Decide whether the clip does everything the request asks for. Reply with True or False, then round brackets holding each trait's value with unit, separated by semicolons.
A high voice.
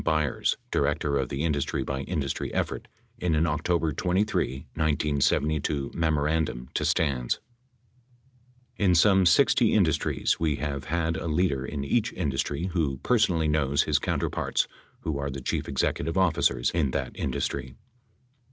False (75 Hz)